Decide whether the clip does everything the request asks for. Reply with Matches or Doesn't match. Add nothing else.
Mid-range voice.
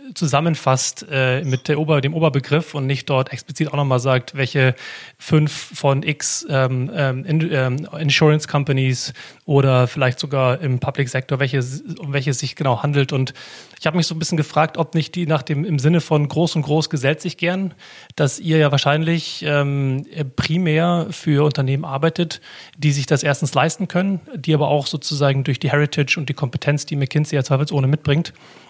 Matches